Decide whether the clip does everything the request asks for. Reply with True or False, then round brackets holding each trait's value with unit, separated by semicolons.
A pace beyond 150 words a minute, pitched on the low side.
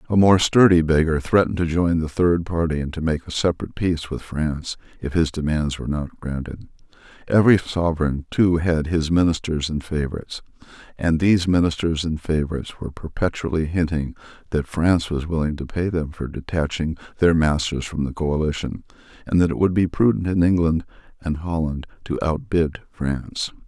True (170 wpm; 80 Hz)